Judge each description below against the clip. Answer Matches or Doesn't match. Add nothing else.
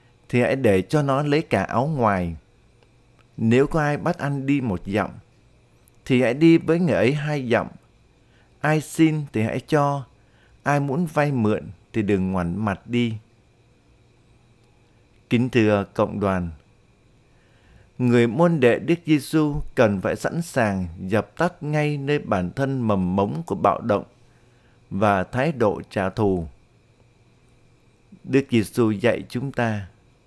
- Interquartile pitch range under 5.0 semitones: Doesn't match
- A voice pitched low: Matches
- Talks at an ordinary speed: Doesn't match